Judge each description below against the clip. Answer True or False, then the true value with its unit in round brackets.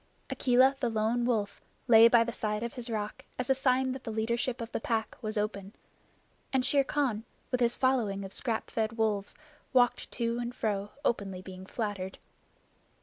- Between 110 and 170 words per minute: False (180 wpm)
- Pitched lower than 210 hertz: False (230 Hz)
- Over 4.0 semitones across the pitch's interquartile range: False (2.8 semitones)